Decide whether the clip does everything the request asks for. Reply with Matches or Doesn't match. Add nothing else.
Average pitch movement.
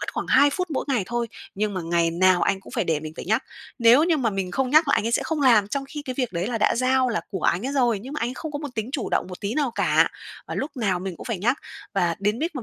Doesn't match